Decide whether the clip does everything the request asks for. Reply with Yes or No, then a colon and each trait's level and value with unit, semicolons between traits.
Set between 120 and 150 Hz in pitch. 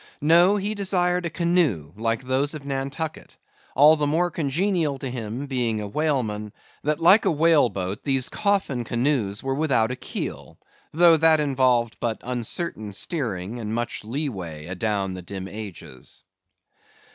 Yes: low, 135 Hz